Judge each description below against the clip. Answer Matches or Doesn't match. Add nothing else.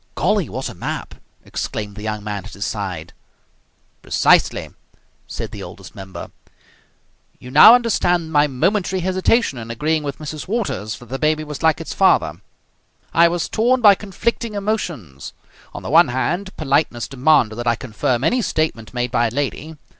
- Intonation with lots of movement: Matches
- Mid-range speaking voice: Matches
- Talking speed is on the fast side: Doesn't match